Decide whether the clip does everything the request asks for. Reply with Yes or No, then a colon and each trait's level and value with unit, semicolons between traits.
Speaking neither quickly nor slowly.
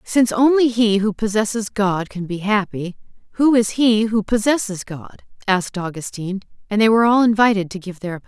Yes: average, 190 wpm